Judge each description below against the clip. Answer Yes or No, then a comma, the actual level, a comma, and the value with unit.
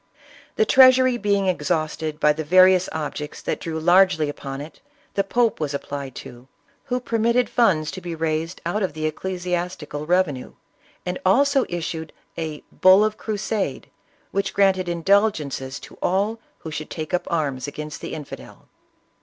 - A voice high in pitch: No, medium, 175 Hz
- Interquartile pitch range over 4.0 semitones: Yes, average, 4.4 semitones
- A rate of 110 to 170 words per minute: Yes, average, 160 wpm